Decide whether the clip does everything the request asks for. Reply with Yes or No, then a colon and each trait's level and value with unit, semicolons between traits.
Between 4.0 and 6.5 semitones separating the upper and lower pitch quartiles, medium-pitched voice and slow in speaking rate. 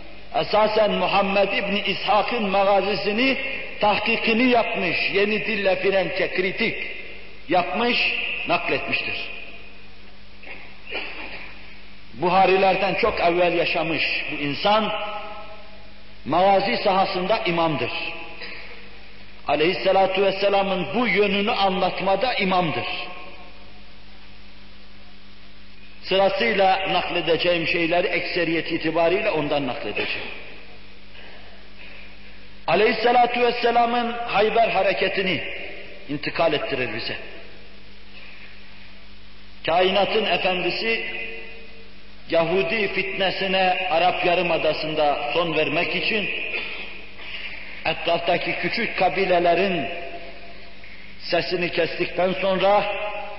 Yes: wide, 5.5 semitones; medium, 180 Hz; slow, 65 wpm